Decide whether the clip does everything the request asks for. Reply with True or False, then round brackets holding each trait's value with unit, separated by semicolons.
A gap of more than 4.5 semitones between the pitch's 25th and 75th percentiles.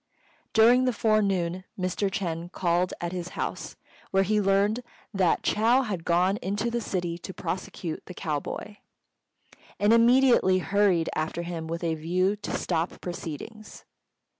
False (3.5 semitones)